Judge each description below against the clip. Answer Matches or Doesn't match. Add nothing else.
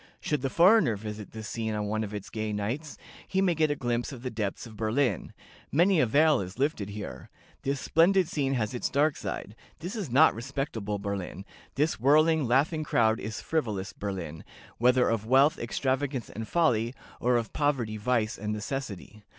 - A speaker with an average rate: Matches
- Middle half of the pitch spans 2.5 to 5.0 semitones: Doesn't match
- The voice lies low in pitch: Matches